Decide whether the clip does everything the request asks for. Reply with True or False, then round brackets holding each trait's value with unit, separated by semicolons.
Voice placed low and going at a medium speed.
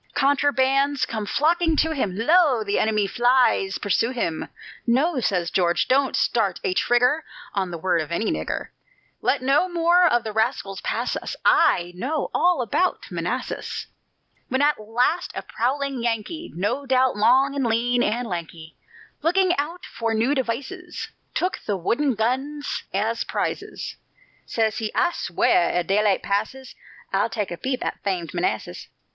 False (240 Hz; 155 wpm)